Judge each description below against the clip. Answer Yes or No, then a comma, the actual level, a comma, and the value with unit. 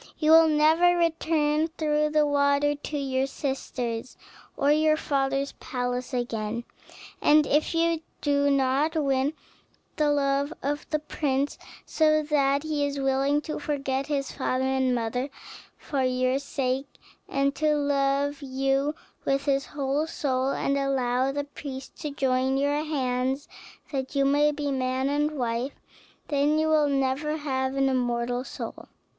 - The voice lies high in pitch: Yes, very high, 280 Hz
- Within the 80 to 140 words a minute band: No, average, 150 wpm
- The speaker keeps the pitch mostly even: Yes, narrow, 2.2 semitones